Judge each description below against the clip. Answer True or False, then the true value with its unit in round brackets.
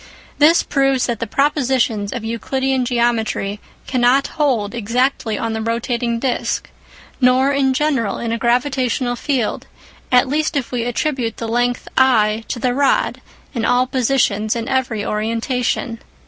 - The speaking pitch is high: True (245 Hz)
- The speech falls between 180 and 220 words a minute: False (145 wpm)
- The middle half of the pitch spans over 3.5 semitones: False (2.6 semitones)